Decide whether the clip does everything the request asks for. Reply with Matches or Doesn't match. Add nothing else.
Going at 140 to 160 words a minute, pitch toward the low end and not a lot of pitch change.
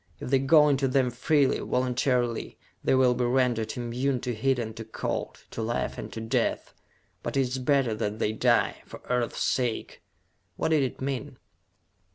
Doesn't match